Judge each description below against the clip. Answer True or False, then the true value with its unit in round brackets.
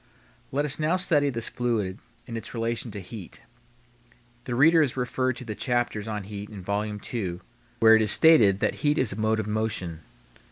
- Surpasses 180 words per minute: True (195 wpm)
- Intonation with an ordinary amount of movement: True (3.6 semitones)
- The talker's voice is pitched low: True (115 Hz)